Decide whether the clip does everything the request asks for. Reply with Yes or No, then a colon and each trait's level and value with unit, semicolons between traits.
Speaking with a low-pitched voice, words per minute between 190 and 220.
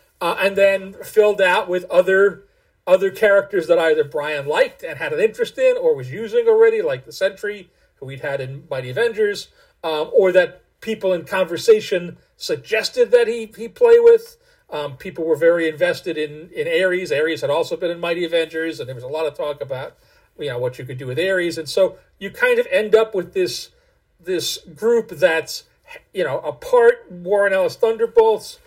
No: high, 200 Hz; average, 195 wpm